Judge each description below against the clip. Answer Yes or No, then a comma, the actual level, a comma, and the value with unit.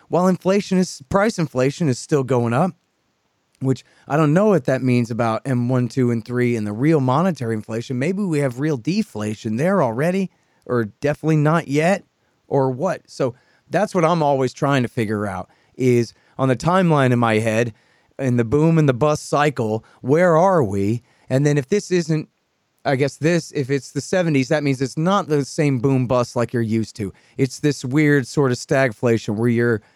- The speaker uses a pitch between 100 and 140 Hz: Yes, low, 135 Hz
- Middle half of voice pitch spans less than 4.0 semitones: No, average, 4.6 semitones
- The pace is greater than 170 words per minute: Yes, average, 195 wpm